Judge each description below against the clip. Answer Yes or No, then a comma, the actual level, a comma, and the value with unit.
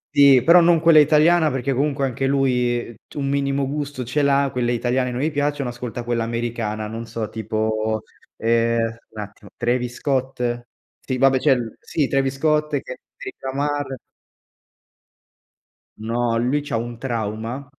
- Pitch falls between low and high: No, low, 125 Hz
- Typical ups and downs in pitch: Yes, average, 3.3 semitones